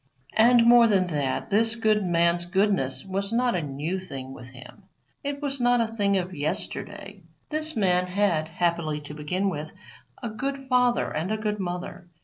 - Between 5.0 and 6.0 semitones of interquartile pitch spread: Yes, wide, 5.4 semitones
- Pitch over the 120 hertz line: Yes, high, 190 Hz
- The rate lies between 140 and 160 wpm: No, average, 175 wpm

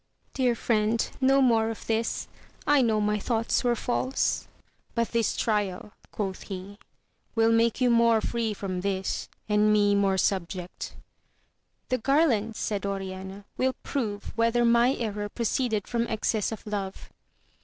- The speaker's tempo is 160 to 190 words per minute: No, average, 150 wpm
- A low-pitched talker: No, high, 220 Hz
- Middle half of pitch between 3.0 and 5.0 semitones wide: No, narrow, 2.6 semitones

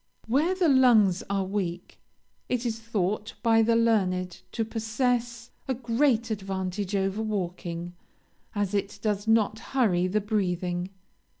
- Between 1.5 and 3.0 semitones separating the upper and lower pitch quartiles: No, average, 3.4 semitones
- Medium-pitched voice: No, high, 215 Hz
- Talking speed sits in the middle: No, slow, 130 wpm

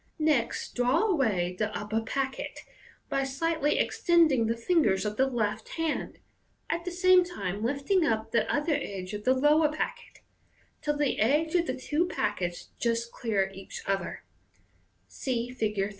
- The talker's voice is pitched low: No, very high, 255 Hz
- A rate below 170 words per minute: Yes, average, 155 wpm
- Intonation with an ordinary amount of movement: No, wide, 6.5 semitones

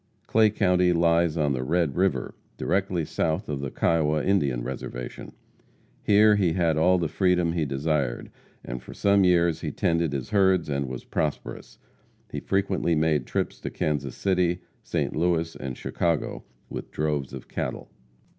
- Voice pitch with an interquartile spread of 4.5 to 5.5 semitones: No, average, 3.8 semitones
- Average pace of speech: Yes, average, 155 wpm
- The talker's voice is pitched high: No, very low, 85 Hz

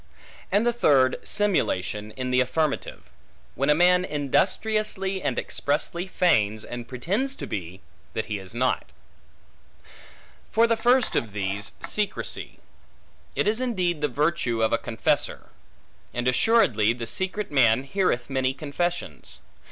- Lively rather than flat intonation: Yes, wide, 8.4 semitones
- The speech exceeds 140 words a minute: No, slow, 135 wpm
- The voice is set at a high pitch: No, medium, 145 Hz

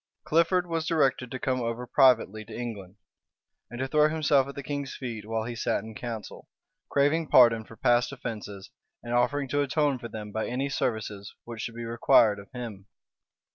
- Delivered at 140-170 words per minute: No, average, 185 wpm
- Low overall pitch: Yes, low, 120 Hz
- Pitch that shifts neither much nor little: Yes, average, 3.9 semitones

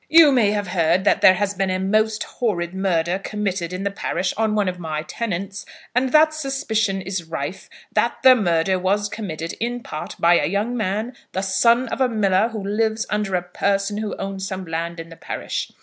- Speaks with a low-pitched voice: No, high, 195 Hz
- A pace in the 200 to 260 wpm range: Yes, fast, 205 wpm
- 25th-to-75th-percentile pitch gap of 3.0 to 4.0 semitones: Yes, average, 3.3 semitones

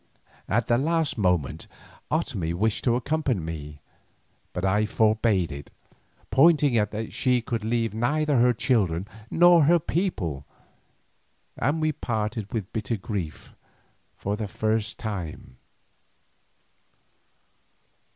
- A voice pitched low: Yes, low, 110 Hz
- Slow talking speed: Yes, slow, 115 wpm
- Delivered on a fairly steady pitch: No, average, 5.2 semitones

